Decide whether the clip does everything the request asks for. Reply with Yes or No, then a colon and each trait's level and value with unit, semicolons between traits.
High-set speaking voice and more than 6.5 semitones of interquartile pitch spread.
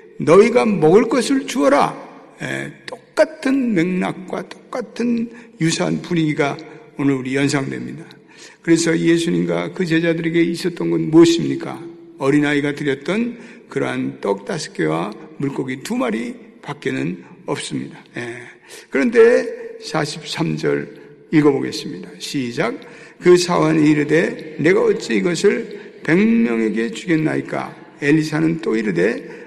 No: medium, 165 Hz; wide, 7.6 semitones